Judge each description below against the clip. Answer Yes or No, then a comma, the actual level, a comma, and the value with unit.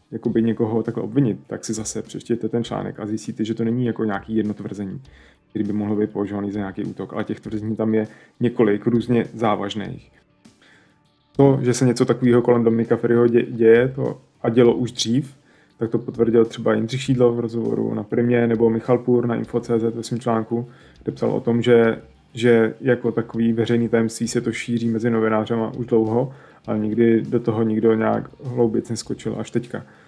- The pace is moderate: No, fast, 190 wpm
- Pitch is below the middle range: Yes, low, 115 Hz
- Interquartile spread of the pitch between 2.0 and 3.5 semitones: No, narrow, 1.4 semitones